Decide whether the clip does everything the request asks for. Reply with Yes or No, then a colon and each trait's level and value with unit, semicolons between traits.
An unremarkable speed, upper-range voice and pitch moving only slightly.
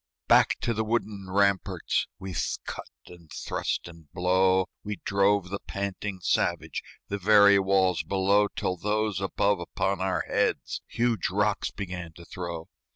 No: average, 145 wpm; very low, 95 Hz; narrow, 1.8 semitones